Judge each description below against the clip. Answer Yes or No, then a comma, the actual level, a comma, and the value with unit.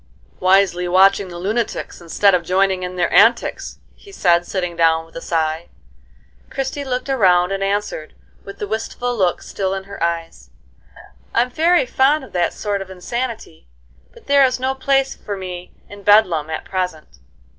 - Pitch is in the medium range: No, high, 195 Hz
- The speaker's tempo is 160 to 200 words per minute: Yes, average, 165 wpm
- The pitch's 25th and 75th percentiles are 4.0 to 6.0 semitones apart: Yes, average, 5.2 semitones